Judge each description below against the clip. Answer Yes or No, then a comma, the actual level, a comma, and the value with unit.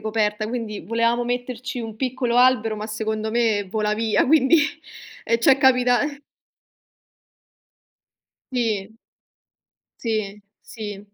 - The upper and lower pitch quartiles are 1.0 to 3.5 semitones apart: Yes, narrow, 2.5 semitones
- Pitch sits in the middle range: No, high, 225 Hz